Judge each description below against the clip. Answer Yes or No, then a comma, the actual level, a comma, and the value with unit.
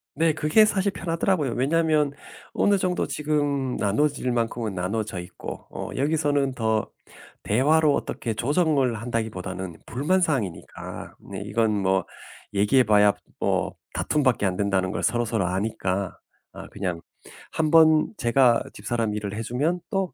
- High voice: No, low, 125 Hz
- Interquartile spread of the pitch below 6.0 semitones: No, wide, 6.7 semitones